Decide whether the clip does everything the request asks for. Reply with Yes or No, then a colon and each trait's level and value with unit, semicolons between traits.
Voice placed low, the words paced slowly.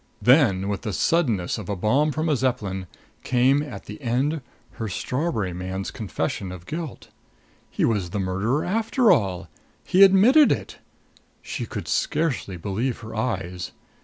No: low, 115 Hz; average, 150 wpm